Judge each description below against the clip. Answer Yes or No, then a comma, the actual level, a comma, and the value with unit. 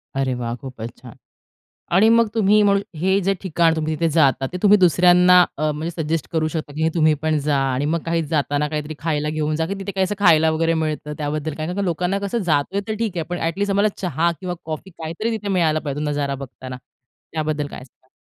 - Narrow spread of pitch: No, average, 3.4 semitones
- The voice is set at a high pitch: No, medium, 160 Hz